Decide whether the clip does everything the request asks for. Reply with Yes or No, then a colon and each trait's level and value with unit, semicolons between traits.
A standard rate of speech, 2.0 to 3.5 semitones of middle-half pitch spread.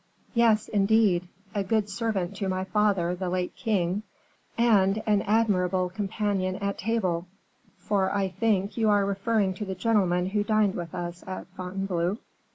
Yes: average, 155 wpm; narrow, 2.5 semitones